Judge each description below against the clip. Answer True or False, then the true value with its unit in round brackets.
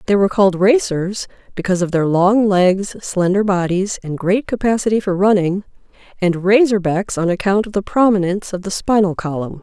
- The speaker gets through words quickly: False (175 wpm)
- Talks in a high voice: True (195 Hz)